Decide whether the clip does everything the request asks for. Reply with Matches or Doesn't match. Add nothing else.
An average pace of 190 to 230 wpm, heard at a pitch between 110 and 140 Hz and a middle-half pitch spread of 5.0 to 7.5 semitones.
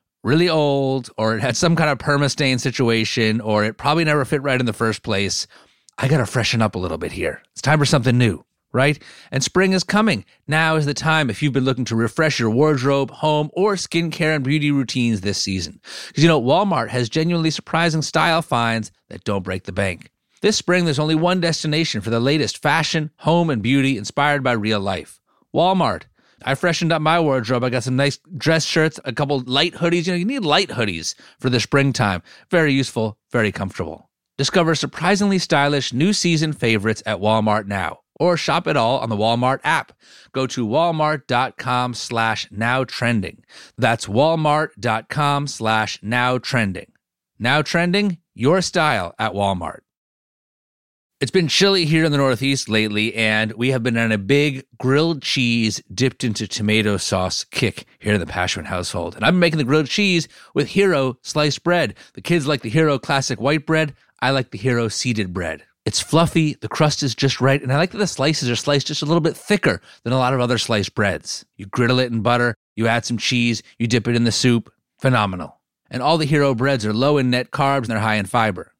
Matches